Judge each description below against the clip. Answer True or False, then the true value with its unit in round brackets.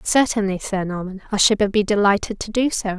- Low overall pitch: False (205 Hz)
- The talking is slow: False (200 wpm)